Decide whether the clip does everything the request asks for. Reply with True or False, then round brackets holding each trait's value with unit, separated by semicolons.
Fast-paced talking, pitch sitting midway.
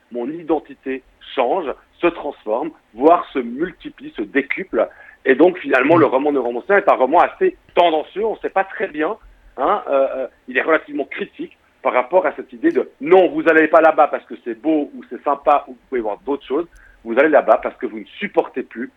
False (210 wpm; 175 Hz)